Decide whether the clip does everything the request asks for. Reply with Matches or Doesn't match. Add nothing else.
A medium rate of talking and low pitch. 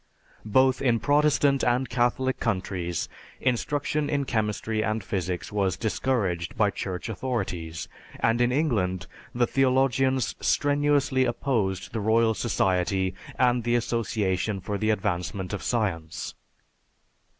Doesn't match